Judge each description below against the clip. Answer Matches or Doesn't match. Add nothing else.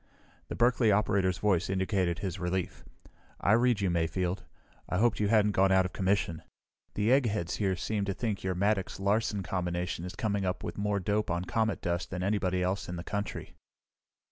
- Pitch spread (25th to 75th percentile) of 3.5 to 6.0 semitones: Doesn't match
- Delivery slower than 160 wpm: Doesn't match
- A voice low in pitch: Matches